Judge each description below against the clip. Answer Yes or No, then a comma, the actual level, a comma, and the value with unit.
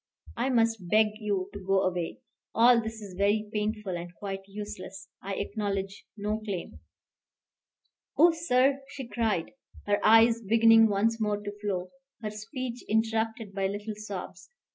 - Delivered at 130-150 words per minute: Yes, average, 145 wpm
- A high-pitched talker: Yes, high, 210 Hz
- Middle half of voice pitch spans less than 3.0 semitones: Yes, narrow, 2.4 semitones